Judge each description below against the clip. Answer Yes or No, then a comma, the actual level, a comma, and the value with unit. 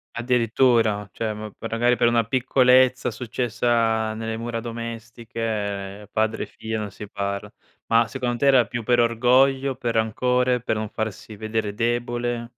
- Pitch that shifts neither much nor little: No, narrow, 1.8 semitones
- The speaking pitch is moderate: No, low, 115 Hz